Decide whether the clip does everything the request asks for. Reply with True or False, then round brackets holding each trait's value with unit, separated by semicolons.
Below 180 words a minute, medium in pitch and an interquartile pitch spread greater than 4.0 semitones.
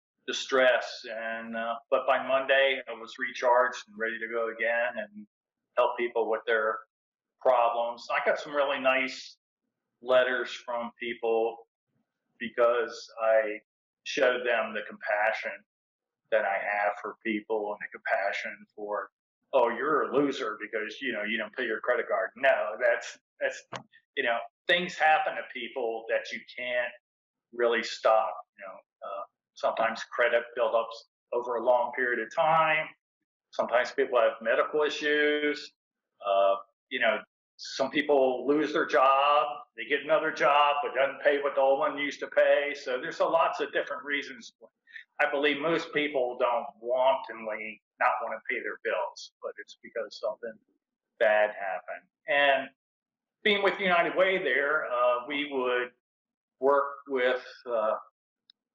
False (150 wpm; 130 Hz; 4.4 semitones)